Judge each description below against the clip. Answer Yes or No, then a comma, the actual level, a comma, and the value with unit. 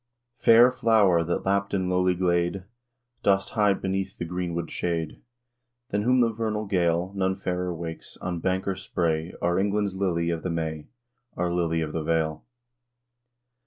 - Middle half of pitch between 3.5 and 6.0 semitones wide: No, narrow, 2.6 semitones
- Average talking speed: Yes, average, 160 wpm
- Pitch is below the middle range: Yes, very low, 90 Hz